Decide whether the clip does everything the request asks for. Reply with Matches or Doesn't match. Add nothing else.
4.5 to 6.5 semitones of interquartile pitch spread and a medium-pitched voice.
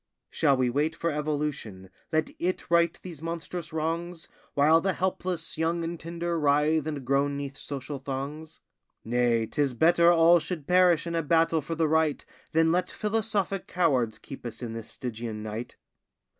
Doesn't match